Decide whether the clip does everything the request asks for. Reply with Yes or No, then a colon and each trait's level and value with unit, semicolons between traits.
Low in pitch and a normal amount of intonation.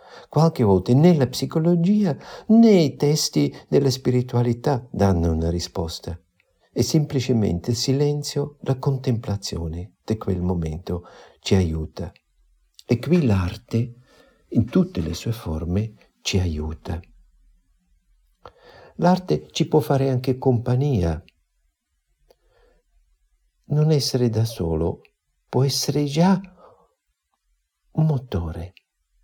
No: low, 115 Hz; wide, 8.6 semitones